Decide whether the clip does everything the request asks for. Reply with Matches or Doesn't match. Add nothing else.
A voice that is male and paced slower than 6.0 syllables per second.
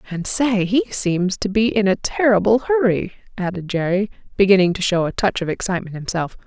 Doesn't match